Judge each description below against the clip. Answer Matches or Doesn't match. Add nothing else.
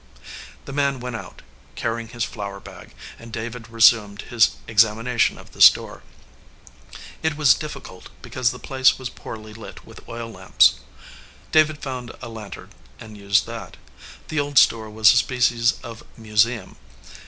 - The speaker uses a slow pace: Doesn't match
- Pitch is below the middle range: Matches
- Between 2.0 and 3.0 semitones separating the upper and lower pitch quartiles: Matches